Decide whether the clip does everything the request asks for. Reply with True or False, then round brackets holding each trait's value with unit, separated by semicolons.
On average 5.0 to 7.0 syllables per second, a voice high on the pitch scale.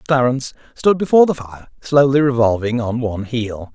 False (5.5 syllables/s; 125 Hz)